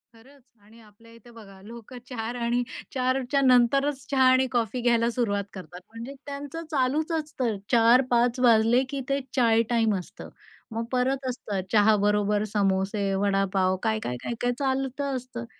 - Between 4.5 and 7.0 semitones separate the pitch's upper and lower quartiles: No, average, 3.4 semitones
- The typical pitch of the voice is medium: No, high, 235 Hz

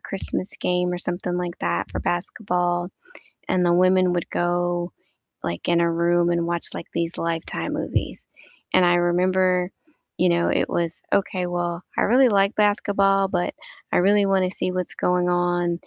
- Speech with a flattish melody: Yes, narrow, 1.2 semitones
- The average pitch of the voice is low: No, medium, 175 Hz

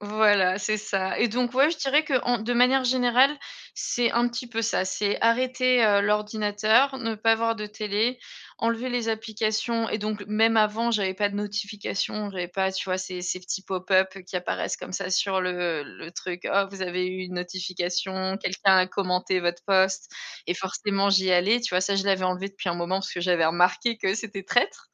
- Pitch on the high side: Yes, high, 205 Hz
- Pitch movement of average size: Yes, average, 3.4 semitones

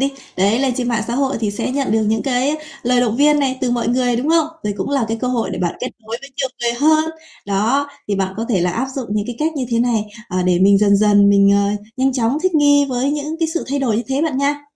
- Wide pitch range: No, average, 4.8 semitones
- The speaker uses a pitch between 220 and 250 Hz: Yes, high, 245 Hz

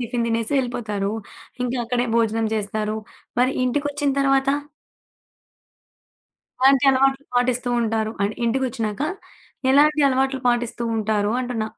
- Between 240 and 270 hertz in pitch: Yes, high, 245 Hz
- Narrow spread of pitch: No, average, 3.4 semitones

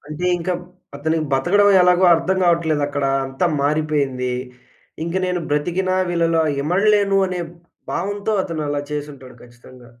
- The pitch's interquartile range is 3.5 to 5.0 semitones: Yes, average, 3.9 semitones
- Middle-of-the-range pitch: Yes, medium, 160 Hz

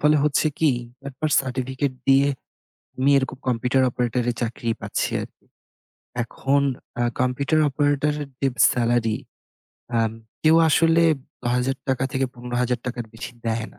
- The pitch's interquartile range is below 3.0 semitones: Yes, narrow, 2.6 semitones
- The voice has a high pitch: No, low, 130 Hz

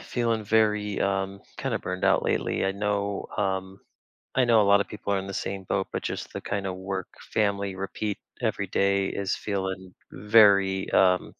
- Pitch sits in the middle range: No, low, 100 Hz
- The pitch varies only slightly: Yes, narrow, 1.4 semitones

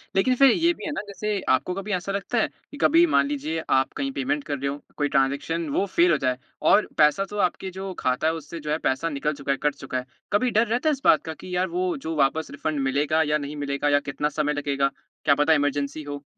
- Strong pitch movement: Yes, wide, 6.2 semitones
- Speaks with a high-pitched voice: No, medium, 160 Hz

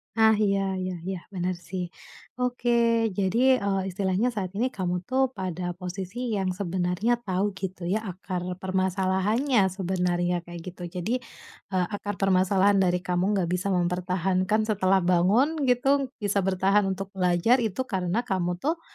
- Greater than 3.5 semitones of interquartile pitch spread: No, average, 3.0 semitones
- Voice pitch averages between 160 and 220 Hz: Yes, high, 190 Hz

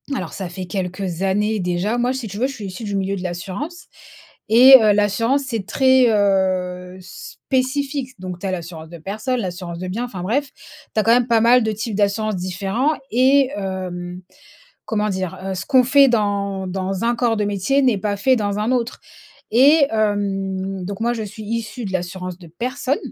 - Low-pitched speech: No, high, 205 Hz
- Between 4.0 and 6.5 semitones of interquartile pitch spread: Yes, average, 4.4 semitones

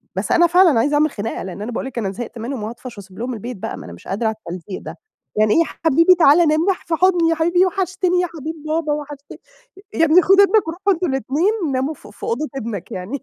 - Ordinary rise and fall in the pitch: No, wide, 7.0 semitones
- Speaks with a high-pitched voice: Yes, very high, 295 Hz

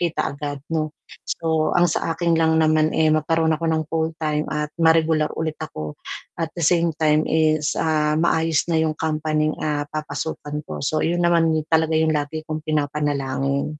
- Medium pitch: Yes, medium, 155 Hz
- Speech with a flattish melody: Yes, narrow, 1.2 semitones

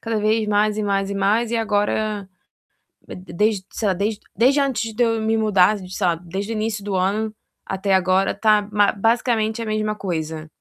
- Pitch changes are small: Yes, narrow, 2.2 semitones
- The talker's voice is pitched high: Yes, high, 210 Hz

